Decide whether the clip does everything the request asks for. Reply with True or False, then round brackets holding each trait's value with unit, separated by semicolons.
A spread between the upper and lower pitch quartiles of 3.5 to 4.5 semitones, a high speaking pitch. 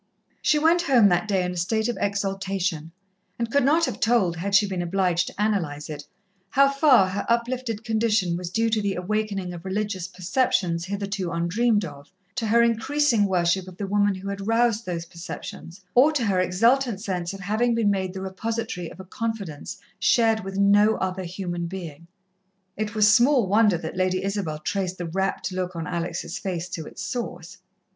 True (3.8 semitones; 195 Hz)